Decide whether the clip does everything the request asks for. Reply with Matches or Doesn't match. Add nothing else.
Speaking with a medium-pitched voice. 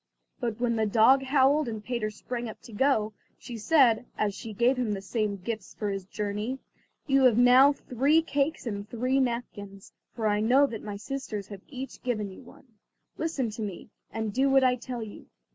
Doesn't match